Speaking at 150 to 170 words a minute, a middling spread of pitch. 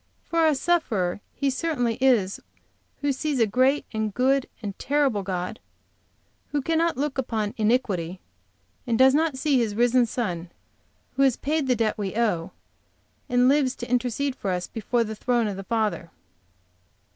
Yes: average, 160 wpm; average, 4.5 semitones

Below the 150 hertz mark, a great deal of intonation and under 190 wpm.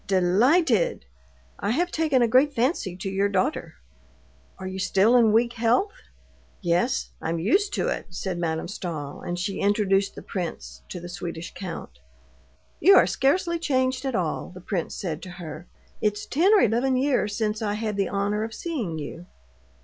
No: high, 205 Hz; wide, 6.3 semitones; average, 170 wpm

